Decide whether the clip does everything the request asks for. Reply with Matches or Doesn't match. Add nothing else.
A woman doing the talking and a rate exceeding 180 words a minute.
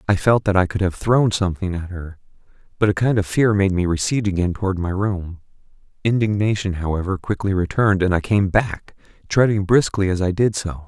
Doesn't match